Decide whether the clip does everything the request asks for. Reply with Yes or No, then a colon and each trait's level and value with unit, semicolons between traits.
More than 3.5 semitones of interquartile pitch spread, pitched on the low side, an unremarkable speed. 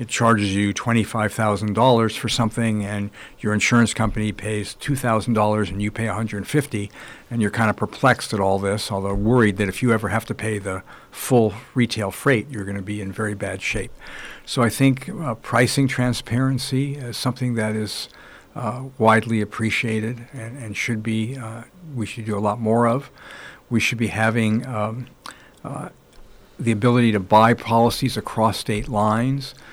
No: narrow, 2.4 semitones; low, 110 Hz; average, 170 wpm